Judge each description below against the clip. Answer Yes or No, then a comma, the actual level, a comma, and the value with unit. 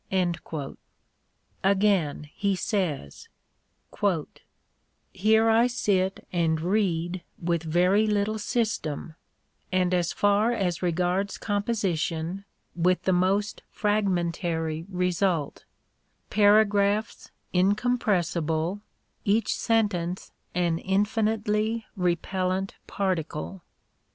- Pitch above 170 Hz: Yes, high, 190 Hz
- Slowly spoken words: Yes, slow, 75 wpm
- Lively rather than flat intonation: No, average, 3.2 semitones